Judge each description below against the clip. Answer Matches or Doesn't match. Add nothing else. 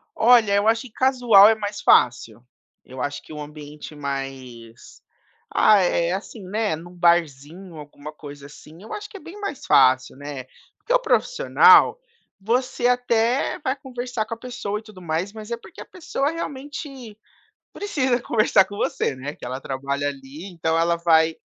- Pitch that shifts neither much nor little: Doesn't match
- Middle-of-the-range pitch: Doesn't match